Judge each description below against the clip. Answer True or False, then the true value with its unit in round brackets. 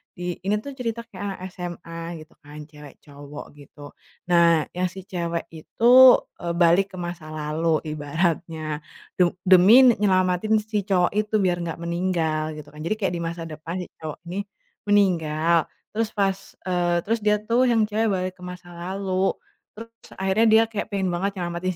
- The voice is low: False (180 Hz)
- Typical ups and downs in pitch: True (3.4 semitones)